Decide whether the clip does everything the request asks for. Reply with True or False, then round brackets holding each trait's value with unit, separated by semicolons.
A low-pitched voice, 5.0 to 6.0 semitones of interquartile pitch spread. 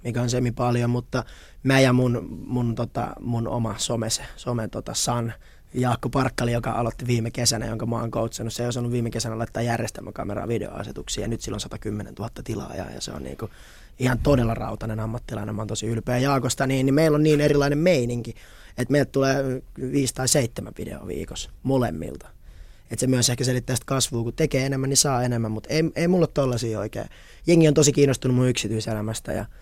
False (120 Hz; 2.9 semitones)